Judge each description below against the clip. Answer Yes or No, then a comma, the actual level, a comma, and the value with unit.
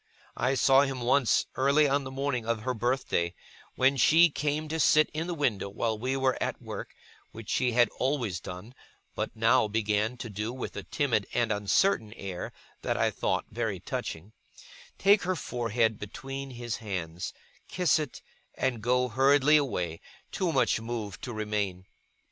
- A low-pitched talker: Yes, low, 120 Hz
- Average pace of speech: Yes, average, 165 wpm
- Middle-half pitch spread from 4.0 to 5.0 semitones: Yes, average, 4.3 semitones